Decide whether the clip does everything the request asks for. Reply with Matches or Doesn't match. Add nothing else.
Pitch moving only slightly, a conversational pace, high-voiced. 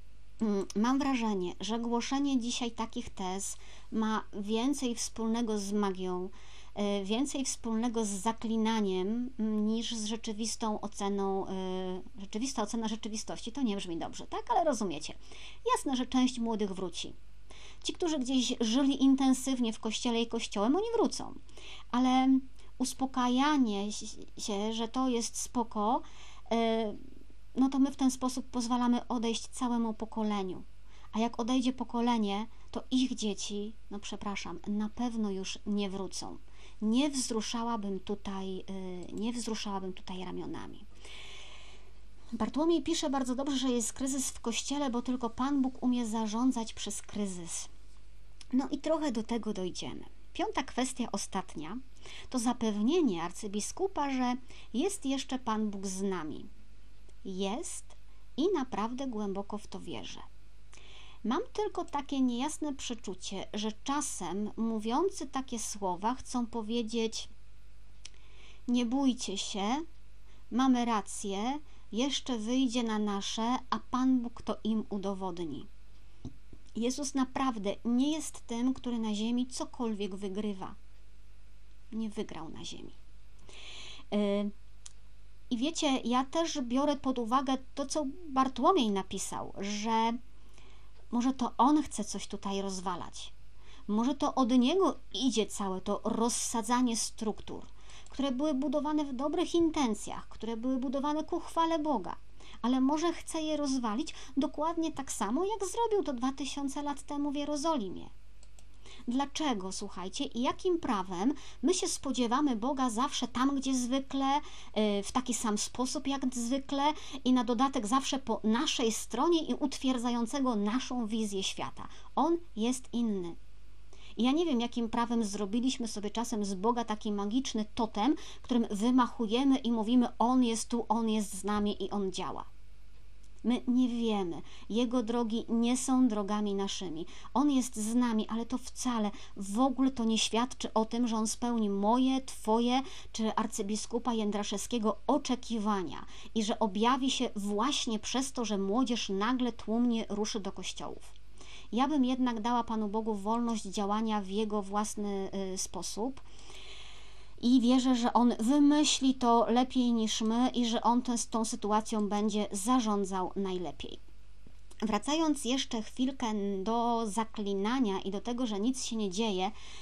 Doesn't match